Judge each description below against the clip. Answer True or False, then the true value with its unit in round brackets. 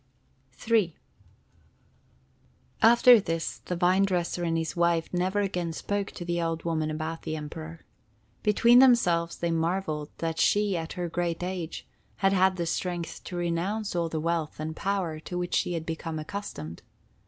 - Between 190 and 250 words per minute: False (160 wpm)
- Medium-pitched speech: True (170 Hz)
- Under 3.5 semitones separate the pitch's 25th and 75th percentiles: True (2.6 semitones)